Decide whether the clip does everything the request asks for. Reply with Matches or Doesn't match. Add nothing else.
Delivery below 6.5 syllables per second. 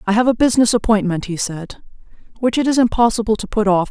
Doesn't match